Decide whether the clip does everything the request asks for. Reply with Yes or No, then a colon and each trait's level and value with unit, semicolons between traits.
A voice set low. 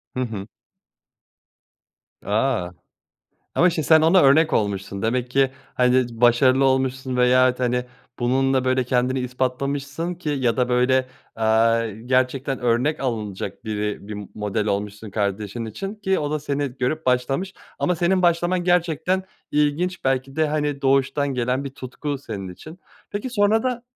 Yes: low, 130 Hz